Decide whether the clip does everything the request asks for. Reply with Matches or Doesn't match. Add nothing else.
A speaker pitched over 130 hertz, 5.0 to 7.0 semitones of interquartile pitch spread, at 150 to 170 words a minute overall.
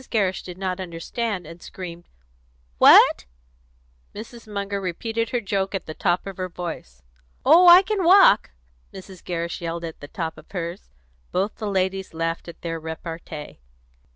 Doesn't match